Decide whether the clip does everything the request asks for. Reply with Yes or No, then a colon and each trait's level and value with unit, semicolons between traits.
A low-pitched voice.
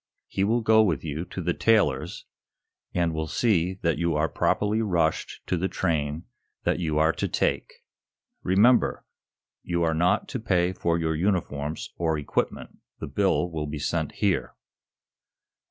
Yes: very low, 85 Hz